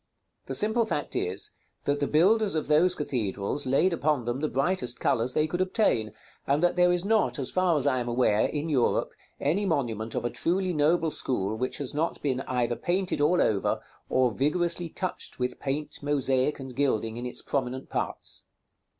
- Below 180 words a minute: No, average, 185 wpm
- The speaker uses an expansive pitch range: Yes, wide, 5.7 semitones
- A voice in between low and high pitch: Yes, medium, 145 Hz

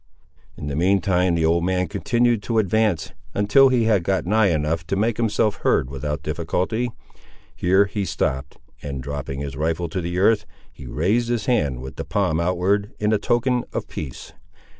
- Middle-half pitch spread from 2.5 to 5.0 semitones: No, wide, 5.5 semitones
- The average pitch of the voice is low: Yes, very low, 90 Hz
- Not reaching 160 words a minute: No, average, 180 wpm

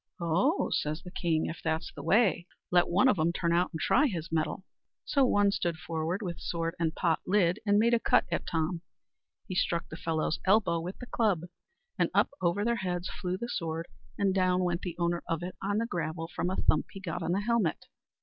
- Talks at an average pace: No, fast, 220 wpm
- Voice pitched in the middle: Yes, medium, 175 Hz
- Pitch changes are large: No, average, 3.1 semitones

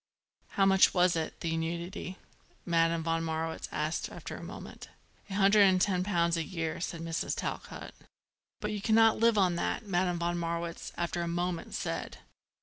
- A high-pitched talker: No, medium, 175 Hz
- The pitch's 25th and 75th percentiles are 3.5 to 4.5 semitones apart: No, narrow, 2.5 semitones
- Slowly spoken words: No, average, 170 wpm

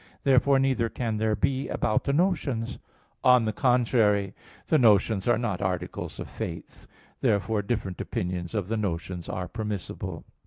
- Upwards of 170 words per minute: No, average, 150 wpm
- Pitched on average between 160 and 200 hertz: No, low, 110 Hz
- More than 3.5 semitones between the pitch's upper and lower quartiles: Yes, average, 4.1 semitones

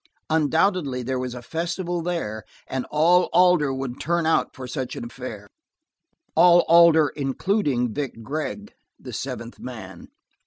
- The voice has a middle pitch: Yes, medium, 150 Hz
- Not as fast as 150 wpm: Yes, average, 140 wpm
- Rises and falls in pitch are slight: No, average, 5.2 semitones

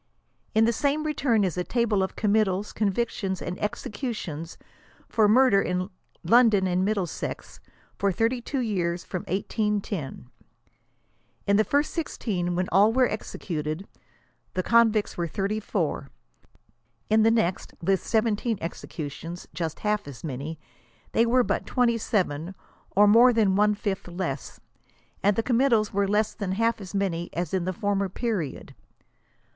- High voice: Yes, high, 200 Hz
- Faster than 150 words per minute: No, average, 145 wpm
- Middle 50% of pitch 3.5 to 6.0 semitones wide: Yes, average, 4.0 semitones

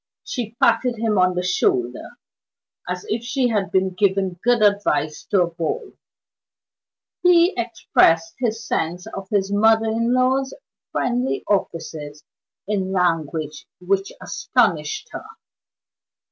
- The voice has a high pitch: Yes, high, 200 Hz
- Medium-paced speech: No, slow, 120 wpm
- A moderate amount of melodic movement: Yes, average, 4.6 semitones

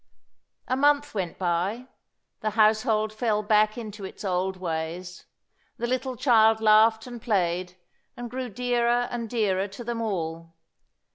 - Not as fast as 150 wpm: Yes, average, 140 wpm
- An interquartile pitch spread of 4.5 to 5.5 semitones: No, average, 4.1 semitones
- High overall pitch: Yes, high, 215 Hz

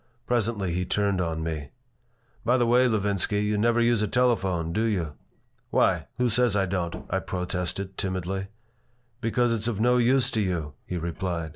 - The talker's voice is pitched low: Yes, low, 100 Hz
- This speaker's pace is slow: No, average, 170 wpm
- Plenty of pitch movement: No, average, 4.5 semitones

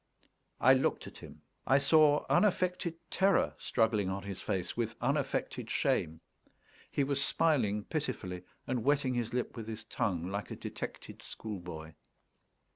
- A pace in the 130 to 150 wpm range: Yes, average, 140 wpm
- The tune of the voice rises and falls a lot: Yes, wide, 6.2 semitones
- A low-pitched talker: Yes, low, 120 Hz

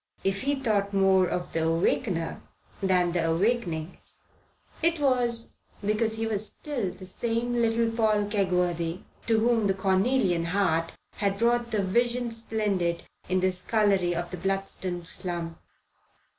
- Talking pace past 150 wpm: No, slow, 135 wpm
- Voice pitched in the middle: No, high, 195 Hz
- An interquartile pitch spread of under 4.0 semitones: No, average, 4.3 semitones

